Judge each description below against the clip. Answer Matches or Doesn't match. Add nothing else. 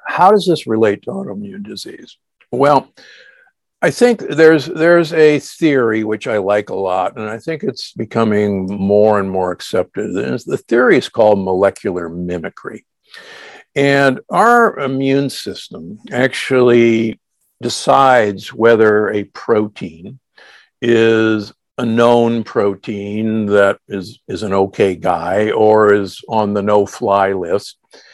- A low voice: Matches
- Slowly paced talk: Matches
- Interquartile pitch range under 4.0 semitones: Doesn't match